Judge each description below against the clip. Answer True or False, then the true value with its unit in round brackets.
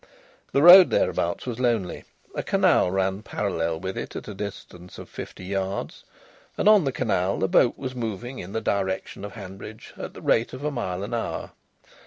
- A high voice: False (100 Hz)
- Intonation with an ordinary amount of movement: True (4.4 semitones)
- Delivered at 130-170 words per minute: False (190 wpm)